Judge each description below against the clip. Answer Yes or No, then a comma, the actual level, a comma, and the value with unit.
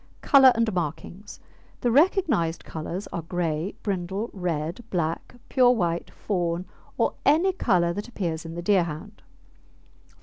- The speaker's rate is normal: No, slow, 130 wpm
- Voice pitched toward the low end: No, medium, 180 Hz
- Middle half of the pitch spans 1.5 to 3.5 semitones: No, wide, 5.4 semitones